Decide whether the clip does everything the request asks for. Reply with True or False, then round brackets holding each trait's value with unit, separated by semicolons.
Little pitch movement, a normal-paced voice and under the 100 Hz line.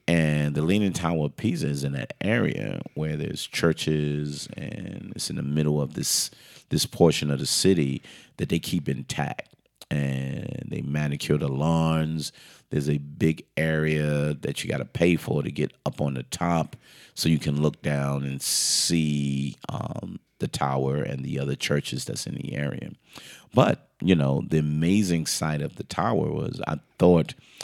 True (1.9 semitones; 175 wpm; 75 Hz)